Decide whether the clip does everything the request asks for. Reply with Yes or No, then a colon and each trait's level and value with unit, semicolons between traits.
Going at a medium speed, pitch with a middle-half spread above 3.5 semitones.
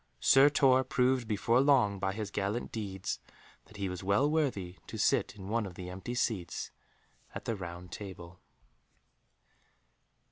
Yes: average, 150 wpm; average, 4.8 semitones